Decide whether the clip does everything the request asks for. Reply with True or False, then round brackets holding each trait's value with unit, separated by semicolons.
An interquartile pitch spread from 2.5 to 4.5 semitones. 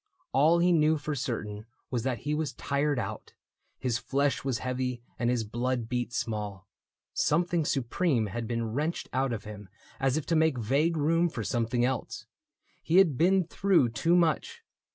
False (5.2 semitones)